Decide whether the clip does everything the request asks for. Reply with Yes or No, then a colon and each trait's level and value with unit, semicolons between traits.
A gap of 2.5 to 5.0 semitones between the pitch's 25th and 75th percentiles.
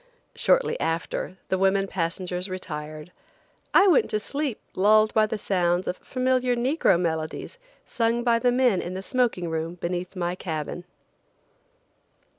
No: wide, 5.4 semitones